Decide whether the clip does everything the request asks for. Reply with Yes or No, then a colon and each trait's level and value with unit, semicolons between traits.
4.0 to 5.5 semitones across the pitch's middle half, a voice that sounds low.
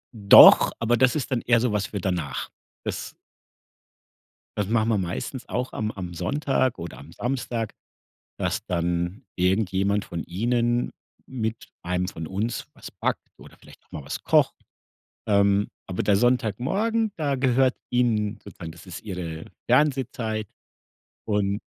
Yes: average, 5.0 semitones; low, 110 Hz